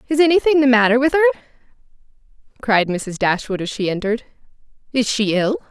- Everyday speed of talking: Yes, average, 145 wpm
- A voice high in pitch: Yes, high, 240 Hz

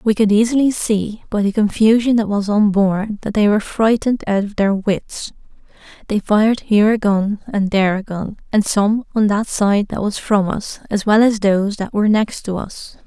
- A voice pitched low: No, high, 210 Hz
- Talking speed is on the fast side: Yes, fast, 210 wpm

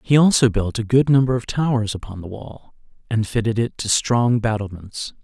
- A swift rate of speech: No, average, 195 wpm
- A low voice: Yes, low, 115 Hz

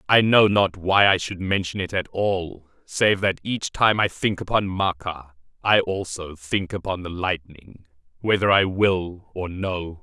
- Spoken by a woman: No, male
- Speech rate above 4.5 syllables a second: No, 4.0 syllables/s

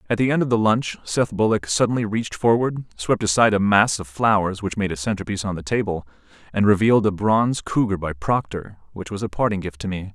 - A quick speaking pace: Yes, fast, 225 wpm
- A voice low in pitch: Yes, low, 105 Hz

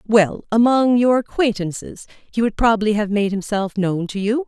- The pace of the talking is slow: No, average, 160 wpm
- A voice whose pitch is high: Yes, high, 215 Hz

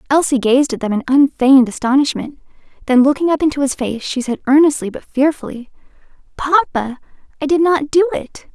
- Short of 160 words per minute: No, average, 170 wpm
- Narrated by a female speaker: Yes, female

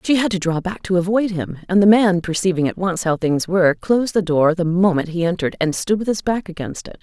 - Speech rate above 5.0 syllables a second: Yes, 5.9 syllables/s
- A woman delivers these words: Yes, female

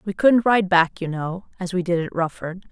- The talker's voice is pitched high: No, medium, 180 Hz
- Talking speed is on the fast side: Yes, fast, 245 wpm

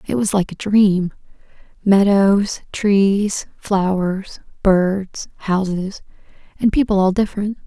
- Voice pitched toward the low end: No, high, 195 Hz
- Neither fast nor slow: No, slow, 100 wpm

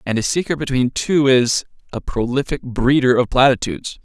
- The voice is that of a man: Yes, male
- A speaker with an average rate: Yes, average, 150 wpm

